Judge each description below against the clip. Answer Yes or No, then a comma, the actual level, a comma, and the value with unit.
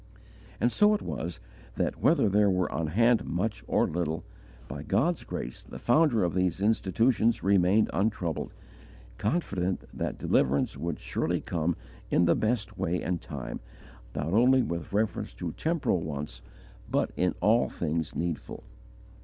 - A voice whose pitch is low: Yes, very low, 90 Hz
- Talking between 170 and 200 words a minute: No, average, 145 wpm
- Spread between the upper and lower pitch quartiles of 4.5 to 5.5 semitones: Yes, average, 5.1 semitones